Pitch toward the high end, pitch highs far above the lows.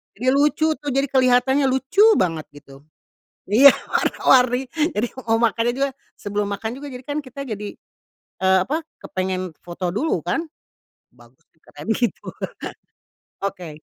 Yes: high, 240 Hz; wide, 6.6 semitones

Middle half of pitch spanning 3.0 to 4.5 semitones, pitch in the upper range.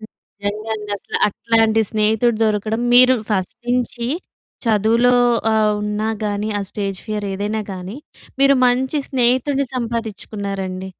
No: narrow, 2.6 semitones; high, 220 Hz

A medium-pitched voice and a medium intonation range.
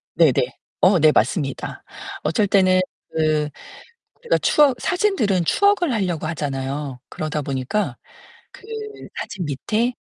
No: medium, 175 Hz; wide, 6.5 semitones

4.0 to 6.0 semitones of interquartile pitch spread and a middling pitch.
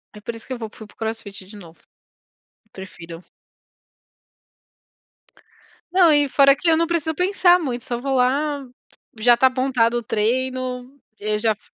No: average, 4.5 semitones; very high, 250 Hz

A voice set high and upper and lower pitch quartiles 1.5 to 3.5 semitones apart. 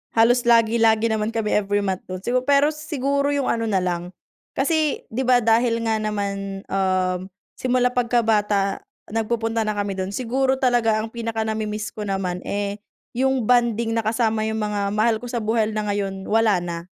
Yes: high, 220 Hz; average, 2.8 semitones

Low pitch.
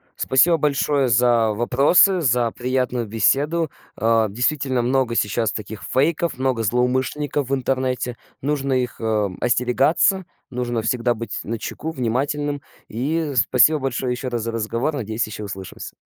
Yes: low, 125 Hz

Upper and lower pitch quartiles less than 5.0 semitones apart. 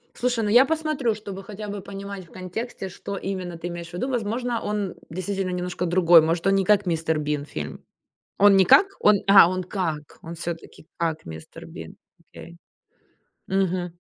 Yes: average, 3.2 semitones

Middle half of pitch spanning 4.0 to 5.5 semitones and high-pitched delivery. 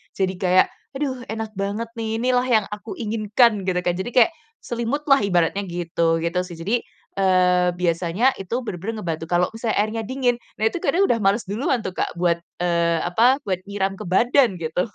Yes: average, 4.6 semitones; high, 200 Hz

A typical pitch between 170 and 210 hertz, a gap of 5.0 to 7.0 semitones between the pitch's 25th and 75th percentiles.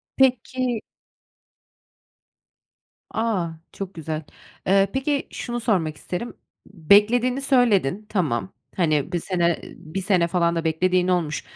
Yes: medium, 185 Hz; wide, 5.4 semitones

